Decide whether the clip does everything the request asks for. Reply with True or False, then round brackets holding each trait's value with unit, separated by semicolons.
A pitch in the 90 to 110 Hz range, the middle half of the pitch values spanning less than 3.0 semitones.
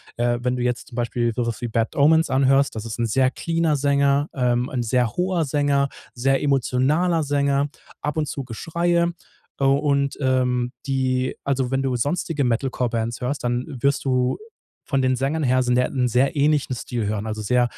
False (130 Hz; 2.5 semitones)